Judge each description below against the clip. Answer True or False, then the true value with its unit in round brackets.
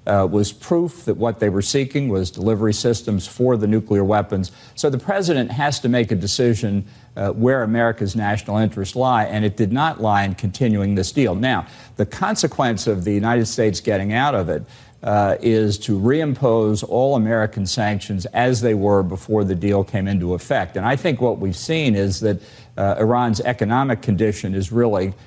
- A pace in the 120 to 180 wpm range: False (190 wpm)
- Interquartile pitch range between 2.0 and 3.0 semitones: False (3.5 semitones)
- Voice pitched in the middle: False (110 Hz)